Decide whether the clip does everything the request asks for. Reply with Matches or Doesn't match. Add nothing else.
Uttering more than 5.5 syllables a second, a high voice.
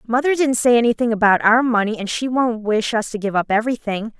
Matches